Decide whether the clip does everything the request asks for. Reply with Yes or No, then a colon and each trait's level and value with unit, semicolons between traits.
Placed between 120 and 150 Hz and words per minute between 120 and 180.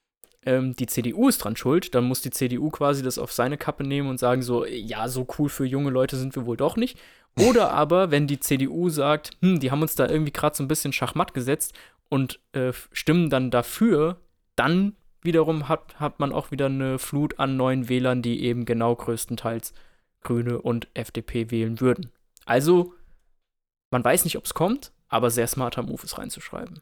No: low, 135 Hz; fast, 190 wpm